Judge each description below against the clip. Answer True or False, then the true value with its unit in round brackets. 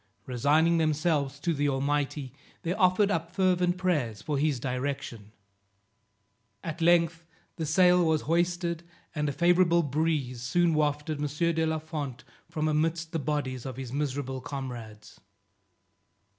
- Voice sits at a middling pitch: True (155 Hz)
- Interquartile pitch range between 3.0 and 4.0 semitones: True (3.4 semitones)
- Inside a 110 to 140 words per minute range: True (135 wpm)